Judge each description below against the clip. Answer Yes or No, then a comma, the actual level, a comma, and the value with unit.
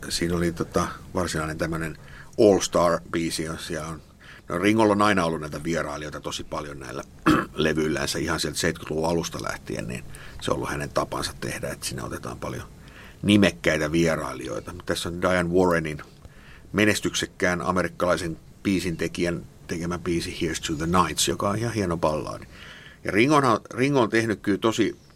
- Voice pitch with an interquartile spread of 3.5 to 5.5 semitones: Yes, average, 4.1 semitones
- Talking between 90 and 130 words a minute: No, average, 145 wpm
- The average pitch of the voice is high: No, very low, 85 Hz